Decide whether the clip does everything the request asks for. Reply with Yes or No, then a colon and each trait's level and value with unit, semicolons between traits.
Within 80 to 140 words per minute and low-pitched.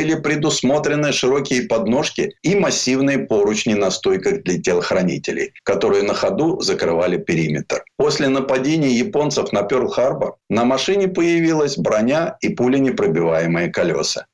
No: average, 115 wpm; medium, 150 Hz